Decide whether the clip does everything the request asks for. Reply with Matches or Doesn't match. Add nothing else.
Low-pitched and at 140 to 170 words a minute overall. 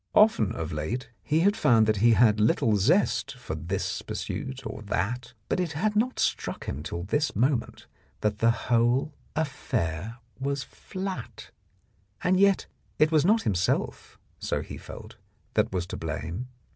Matches